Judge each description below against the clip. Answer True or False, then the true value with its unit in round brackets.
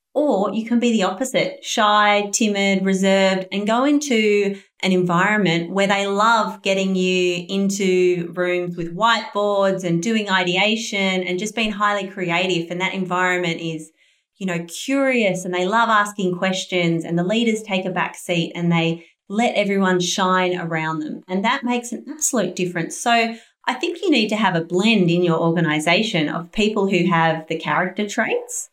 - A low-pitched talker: False (190 Hz)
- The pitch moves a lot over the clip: False (3.5 semitones)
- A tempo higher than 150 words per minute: True (170 wpm)